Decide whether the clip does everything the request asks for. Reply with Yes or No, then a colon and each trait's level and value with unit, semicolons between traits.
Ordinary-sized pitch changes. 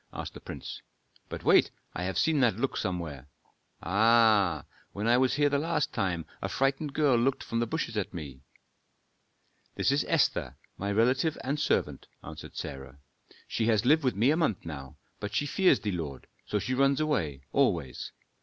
No: wide, 7.5 semitones